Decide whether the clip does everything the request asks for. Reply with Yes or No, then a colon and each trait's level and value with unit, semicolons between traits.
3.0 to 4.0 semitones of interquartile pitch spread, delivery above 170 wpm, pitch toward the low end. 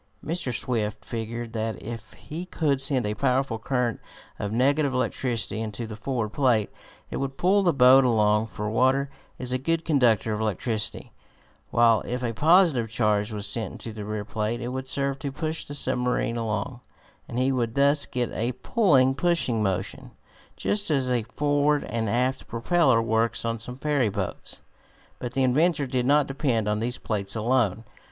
Yes: average, 3.6 semitones; average, 180 wpm; low, 125 Hz